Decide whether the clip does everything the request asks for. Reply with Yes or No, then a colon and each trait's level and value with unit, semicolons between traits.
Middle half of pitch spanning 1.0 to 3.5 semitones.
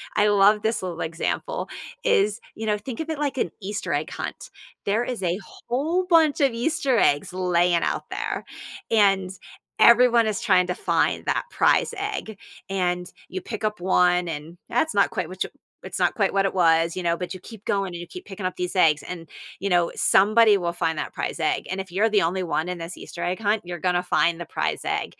No: average, 4.1 semitones